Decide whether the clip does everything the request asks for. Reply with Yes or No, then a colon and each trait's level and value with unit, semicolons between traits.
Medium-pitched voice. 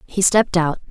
Yes: medium, 180 Hz